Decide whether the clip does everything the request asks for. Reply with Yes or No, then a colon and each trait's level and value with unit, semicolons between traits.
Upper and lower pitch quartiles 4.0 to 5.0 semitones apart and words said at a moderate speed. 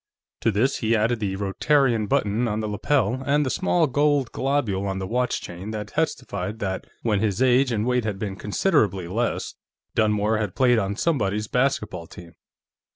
Yes: average, 4.3 semitones; average, 175 wpm